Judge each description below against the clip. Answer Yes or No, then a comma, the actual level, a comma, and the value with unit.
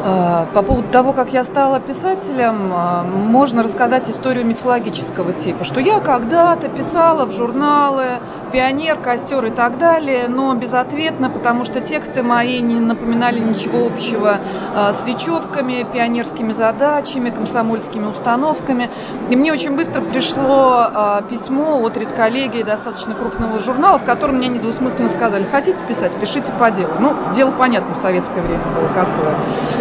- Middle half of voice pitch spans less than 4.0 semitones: Yes, average, 3.1 semitones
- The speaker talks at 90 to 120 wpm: No, average, 135 wpm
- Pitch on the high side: Yes, high, 245 Hz